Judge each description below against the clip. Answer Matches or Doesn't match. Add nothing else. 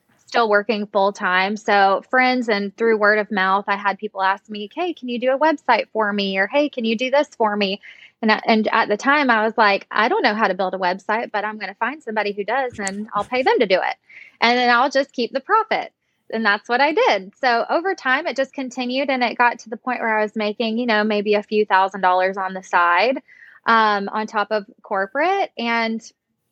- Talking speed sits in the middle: Doesn't match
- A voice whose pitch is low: Doesn't match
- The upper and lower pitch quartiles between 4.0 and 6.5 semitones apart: Doesn't match